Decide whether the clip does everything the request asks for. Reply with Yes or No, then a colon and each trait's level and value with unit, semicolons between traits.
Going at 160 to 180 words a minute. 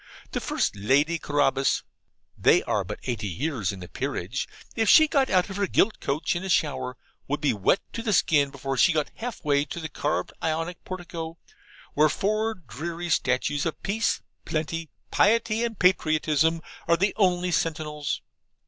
Yes: average, 170 wpm